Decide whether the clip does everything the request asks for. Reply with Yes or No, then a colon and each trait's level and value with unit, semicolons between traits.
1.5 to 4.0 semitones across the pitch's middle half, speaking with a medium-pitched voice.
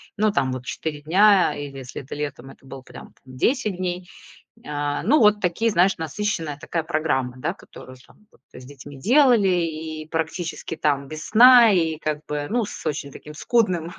No: wide, 5.6 semitones; medium, 160 Hz